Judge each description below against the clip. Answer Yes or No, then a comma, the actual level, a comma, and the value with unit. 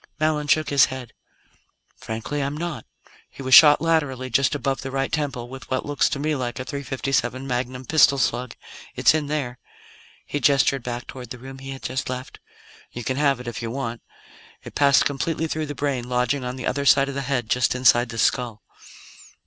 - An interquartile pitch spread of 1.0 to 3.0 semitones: Yes, narrow, 2.4 semitones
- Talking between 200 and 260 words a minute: Yes, fast, 205 wpm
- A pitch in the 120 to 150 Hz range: Yes, low, 135 Hz